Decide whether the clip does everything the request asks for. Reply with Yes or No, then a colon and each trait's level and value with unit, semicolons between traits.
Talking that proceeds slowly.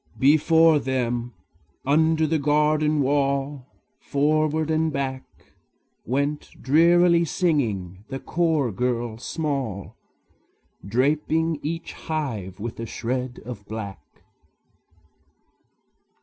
Yes: slow, 90 wpm